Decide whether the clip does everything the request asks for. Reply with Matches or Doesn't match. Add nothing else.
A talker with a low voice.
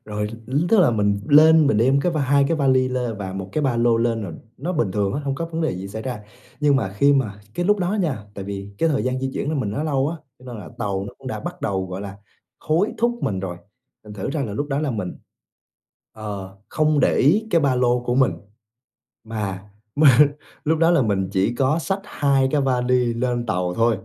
Matches